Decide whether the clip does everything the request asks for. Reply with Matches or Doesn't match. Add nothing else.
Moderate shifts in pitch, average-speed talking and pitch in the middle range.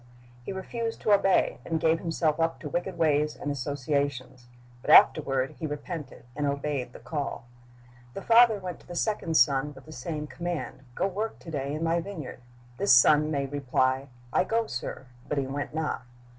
Matches